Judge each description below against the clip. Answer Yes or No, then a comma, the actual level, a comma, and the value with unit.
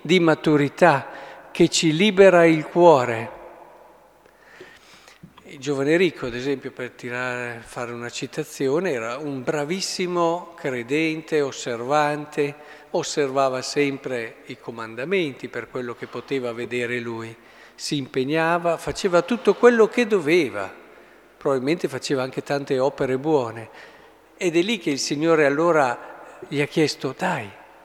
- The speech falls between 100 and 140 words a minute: Yes, average, 120 wpm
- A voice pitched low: No, medium, 150 Hz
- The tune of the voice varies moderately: Yes, average, 4.2 semitones